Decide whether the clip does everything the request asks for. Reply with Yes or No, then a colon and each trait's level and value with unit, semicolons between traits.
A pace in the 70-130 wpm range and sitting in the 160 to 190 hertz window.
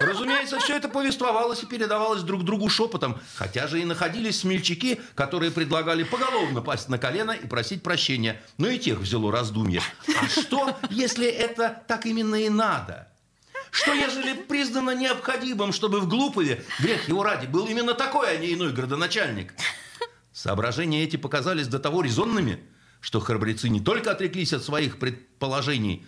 No: average, 155 wpm; medium, 185 Hz